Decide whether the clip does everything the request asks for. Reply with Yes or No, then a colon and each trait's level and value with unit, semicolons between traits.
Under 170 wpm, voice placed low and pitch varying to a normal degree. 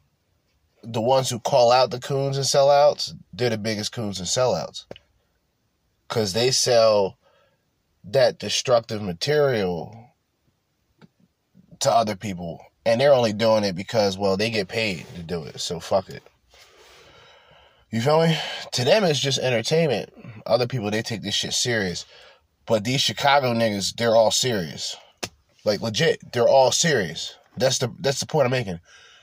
Yes: average, 150 wpm; low, 115 Hz; average, 4.5 semitones